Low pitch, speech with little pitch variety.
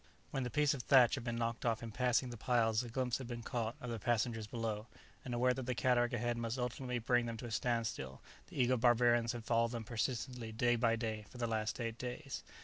Yes: low, 120 Hz; narrow, 1.4 semitones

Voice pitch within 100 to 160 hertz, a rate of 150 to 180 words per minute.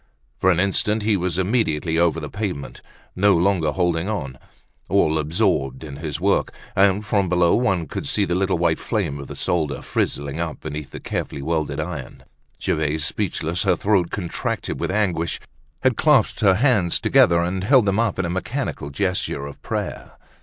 No: very low, 90 Hz; average, 175 wpm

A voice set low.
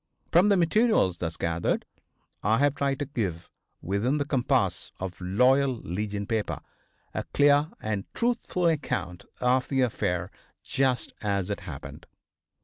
Yes: low, 125 Hz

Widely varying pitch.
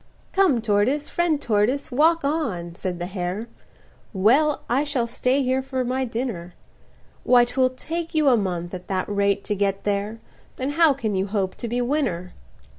Yes: wide, 5.8 semitones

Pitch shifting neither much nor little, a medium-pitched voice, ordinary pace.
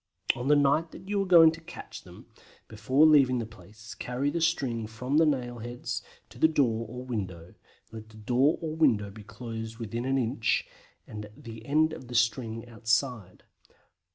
No: average, 4.5 semitones; low, 120 Hz; average, 180 wpm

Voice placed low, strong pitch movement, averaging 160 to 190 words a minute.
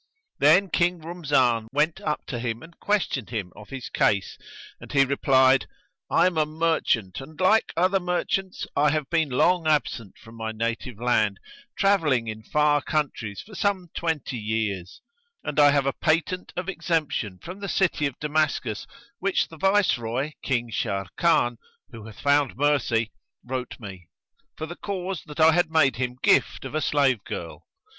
No: medium, 145 Hz; wide, 6.2 semitones; average, 165 wpm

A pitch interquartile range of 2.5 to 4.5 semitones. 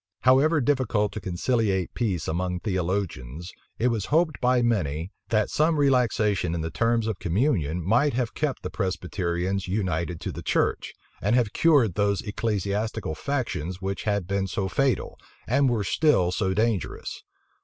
No: average, 5.1 semitones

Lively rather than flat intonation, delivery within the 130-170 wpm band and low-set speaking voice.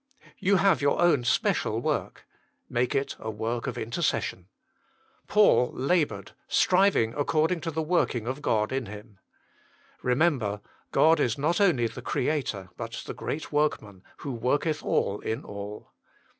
Yes: wide, 6.1 semitones; average, 145 wpm; low, 130 Hz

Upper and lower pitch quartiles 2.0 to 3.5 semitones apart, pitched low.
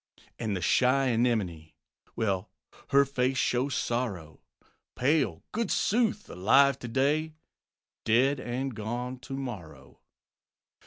No: average, 3.9 semitones; low, 125 Hz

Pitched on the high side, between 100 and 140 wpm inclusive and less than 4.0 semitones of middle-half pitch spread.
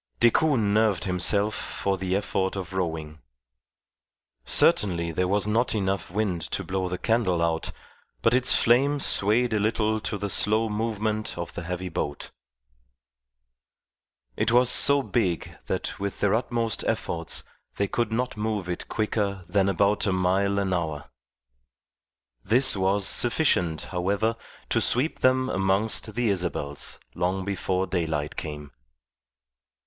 No: low, 100 Hz; slow, 135 wpm; average, 3.4 semitones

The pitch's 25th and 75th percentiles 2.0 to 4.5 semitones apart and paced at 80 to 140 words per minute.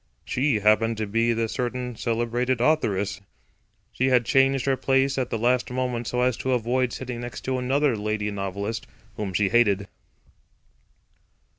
No: average, 3.0 semitones; average, 155 wpm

